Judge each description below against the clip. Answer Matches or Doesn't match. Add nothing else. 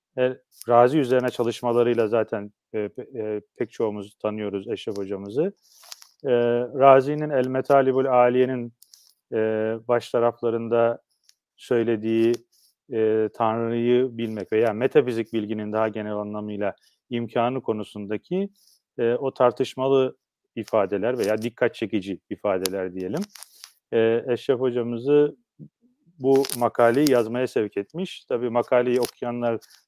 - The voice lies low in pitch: Matches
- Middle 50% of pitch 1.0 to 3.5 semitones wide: Matches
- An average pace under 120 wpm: Matches